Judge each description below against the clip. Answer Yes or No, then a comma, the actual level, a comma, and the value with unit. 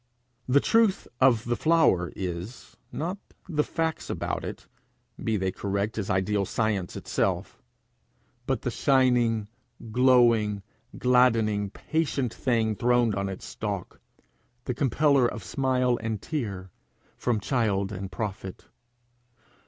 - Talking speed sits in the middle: No, slow, 120 wpm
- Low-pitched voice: Yes, low, 115 Hz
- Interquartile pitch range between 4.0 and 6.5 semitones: Yes, average, 4.3 semitones